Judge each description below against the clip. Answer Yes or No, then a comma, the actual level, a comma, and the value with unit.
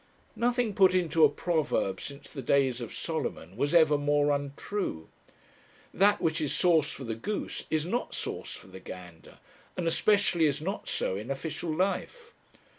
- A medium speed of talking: Yes, average, 165 wpm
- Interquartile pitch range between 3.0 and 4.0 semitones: No, average, 5.1 semitones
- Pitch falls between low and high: Yes, medium, 155 Hz